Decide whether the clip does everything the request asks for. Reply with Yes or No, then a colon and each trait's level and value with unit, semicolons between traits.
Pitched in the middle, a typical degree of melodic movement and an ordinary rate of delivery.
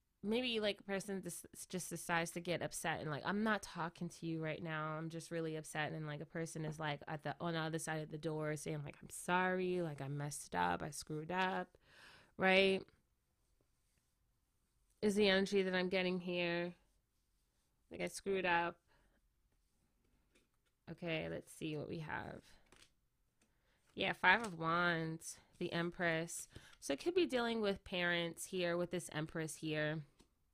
Yes: medium, 170 Hz; average, 3.0 semitones; average, 165 wpm